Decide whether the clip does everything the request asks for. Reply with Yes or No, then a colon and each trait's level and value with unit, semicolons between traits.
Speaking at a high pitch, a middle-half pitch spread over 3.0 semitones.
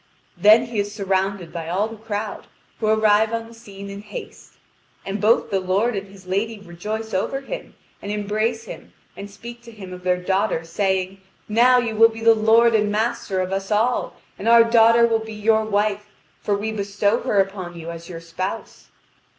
No: high, 210 Hz; narrow, 2.5 semitones